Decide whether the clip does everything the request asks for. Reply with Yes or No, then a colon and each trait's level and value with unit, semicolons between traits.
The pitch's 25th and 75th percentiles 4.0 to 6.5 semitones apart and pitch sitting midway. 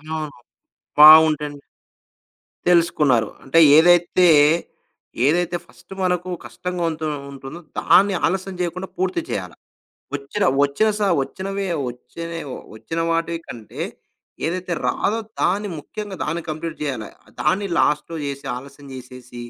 Yes: average, 4.3 semitones; medium, 165 Hz